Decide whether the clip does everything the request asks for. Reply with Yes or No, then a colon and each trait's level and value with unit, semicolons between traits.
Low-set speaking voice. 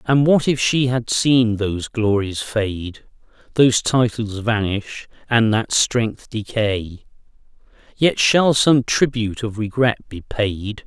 Yes: low, 115 Hz